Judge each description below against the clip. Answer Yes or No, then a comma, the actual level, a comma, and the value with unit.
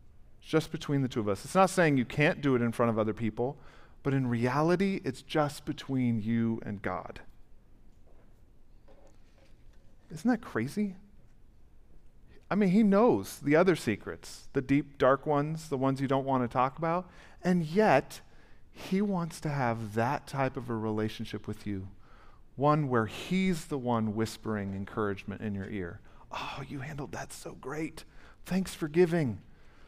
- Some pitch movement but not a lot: No, wide, 6.0 semitones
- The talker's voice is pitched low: Yes, low, 130 Hz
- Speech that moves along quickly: No, average, 165 wpm